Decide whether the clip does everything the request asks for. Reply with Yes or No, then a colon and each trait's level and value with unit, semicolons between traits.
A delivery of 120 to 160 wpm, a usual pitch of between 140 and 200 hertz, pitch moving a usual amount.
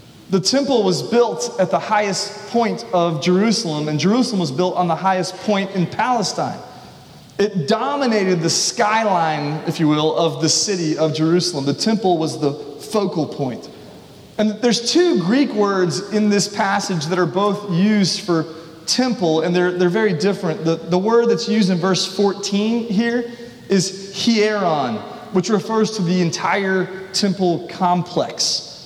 Yes: average, 155 wpm; high, 190 Hz; average, 3.8 semitones